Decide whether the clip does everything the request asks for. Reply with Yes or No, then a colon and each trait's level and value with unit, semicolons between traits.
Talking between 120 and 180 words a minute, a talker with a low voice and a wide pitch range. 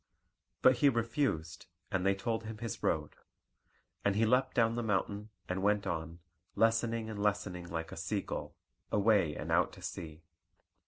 No: average, 165 wpm; low, 105 Hz; average, 4.1 semitones